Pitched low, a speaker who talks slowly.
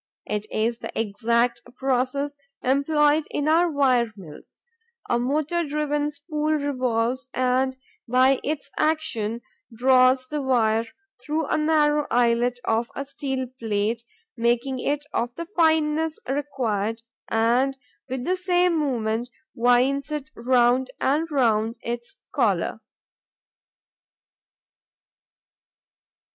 No: very high, 260 Hz; slow, 110 wpm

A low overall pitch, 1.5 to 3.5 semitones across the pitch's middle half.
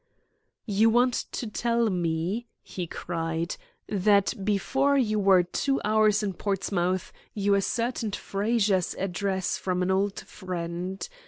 No: high, 200 Hz; average, 3.0 semitones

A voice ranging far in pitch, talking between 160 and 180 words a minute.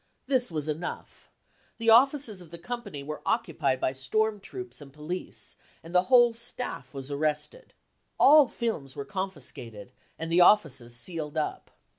No: wide, 8.2 semitones; average, 150 wpm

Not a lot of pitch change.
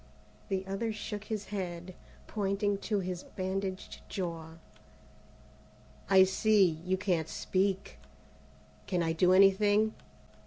Yes: narrow, 2.0 semitones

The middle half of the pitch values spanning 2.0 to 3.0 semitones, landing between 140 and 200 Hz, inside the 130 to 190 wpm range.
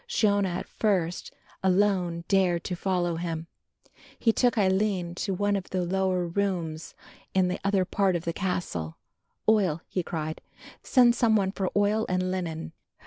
Yes: average, 2.7 semitones; medium, 185 Hz; average, 155 wpm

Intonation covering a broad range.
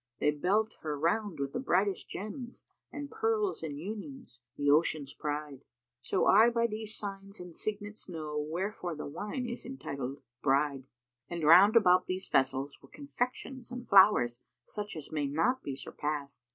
Yes: wide, 7.1 semitones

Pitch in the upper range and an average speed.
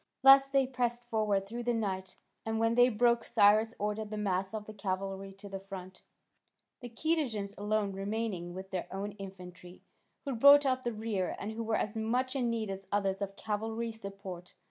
Yes: high, 210 Hz; average, 190 wpm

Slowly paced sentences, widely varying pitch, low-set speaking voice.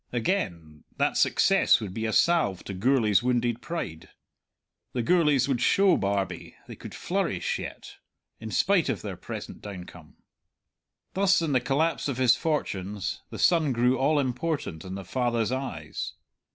No: average, 150 wpm; wide, 6.9 semitones; low, 120 Hz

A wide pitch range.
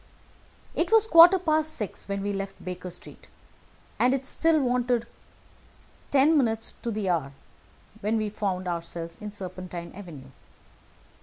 Yes: wide, 6.8 semitones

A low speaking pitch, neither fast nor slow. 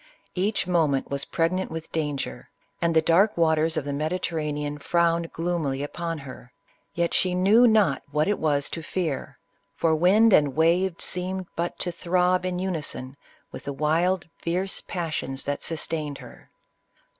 No: medium, 165 Hz; average, 155 wpm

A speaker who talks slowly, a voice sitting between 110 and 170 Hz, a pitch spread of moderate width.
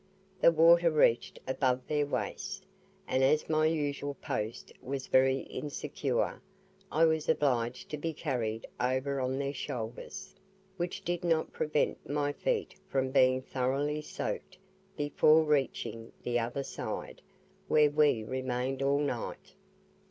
Yes: slow, 130 wpm; medium, 140 Hz; average, 3.0 semitones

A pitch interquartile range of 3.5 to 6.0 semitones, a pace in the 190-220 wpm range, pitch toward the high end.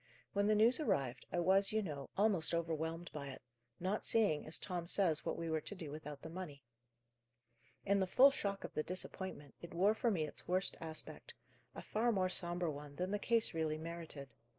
No: average, 4.3 semitones; average, 200 wpm; medium, 175 Hz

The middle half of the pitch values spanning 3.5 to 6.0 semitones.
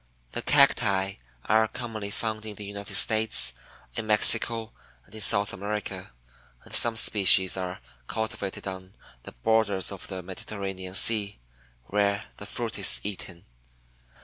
No: narrow, 2.5 semitones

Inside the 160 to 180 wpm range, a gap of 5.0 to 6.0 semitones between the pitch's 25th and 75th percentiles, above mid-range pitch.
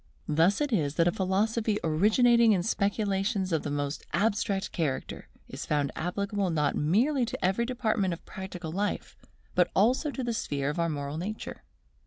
Yes: average, 170 wpm; average, 5.3 semitones; high, 195 Hz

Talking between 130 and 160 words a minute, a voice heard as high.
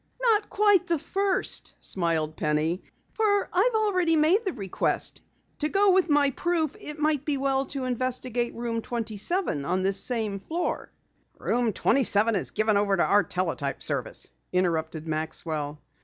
Yes: average, 155 wpm; high, 245 Hz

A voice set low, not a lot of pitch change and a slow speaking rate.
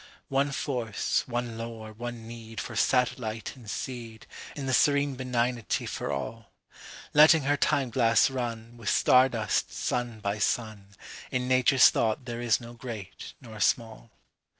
Yes: low, 120 Hz; narrow, 2.3 semitones; slow, 125 wpm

